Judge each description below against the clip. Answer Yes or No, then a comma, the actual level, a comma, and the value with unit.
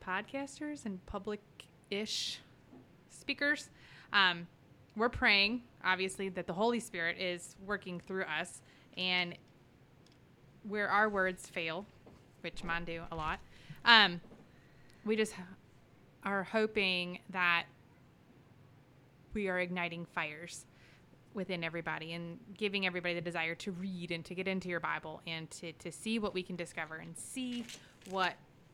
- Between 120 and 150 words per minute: Yes, slow, 135 wpm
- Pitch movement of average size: Yes, average, 3.7 semitones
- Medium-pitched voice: Yes, medium, 180 Hz